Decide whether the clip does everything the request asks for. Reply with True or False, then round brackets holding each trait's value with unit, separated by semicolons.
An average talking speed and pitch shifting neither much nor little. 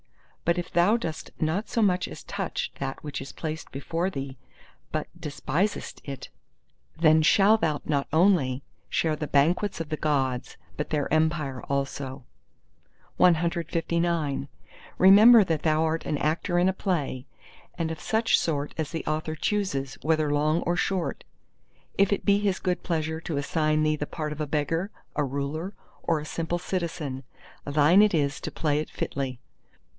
True (165 wpm; 3.1 semitones)